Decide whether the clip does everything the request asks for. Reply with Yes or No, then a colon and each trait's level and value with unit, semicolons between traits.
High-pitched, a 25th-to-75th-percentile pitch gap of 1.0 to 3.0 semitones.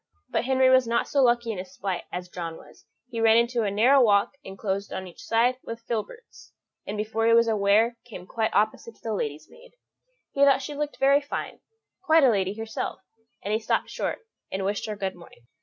No: high, 225 Hz; average, 3.9 semitones